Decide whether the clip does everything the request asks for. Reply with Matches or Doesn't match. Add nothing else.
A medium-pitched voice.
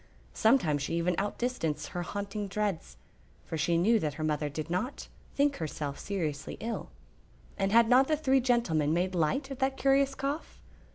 Doesn't match